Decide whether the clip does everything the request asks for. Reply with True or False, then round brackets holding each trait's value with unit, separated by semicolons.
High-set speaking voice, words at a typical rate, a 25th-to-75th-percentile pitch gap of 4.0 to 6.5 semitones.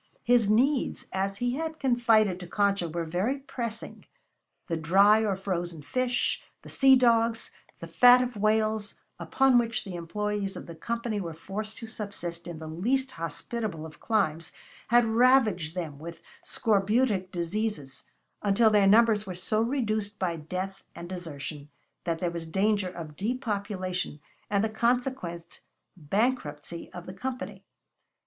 True (205 Hz; 145 wpm; 5.2 semitones)